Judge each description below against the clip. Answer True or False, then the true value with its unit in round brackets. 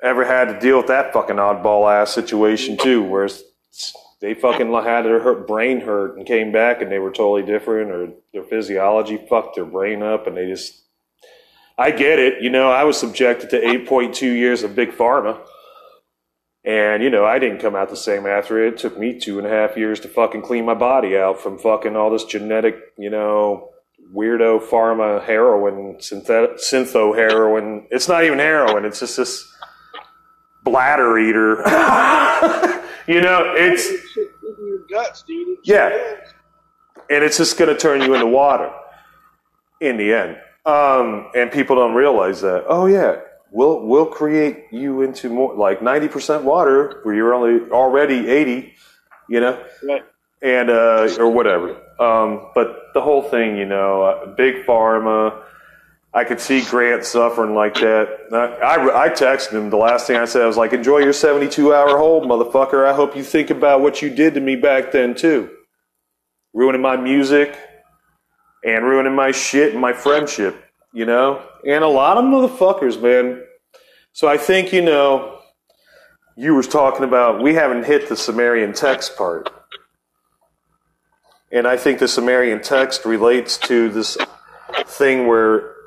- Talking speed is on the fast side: False (165 wpm)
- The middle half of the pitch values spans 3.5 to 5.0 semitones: True (4.7 semitones)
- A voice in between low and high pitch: False (125 Hz)